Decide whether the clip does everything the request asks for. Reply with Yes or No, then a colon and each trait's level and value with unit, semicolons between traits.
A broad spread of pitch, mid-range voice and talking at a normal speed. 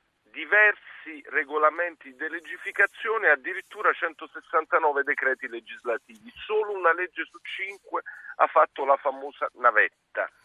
No: wide, 5.8 semitones; medium, 160 Hz; slow, 110 wpm